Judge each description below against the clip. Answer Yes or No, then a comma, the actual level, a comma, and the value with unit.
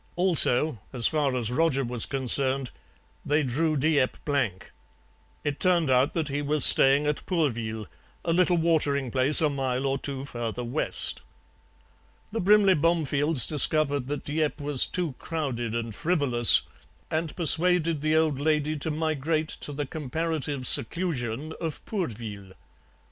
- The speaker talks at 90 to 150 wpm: Yes, average, 140 wpm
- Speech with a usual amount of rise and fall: Yes, average, 3.7 semitones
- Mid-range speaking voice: Yes, medium, 145 Hz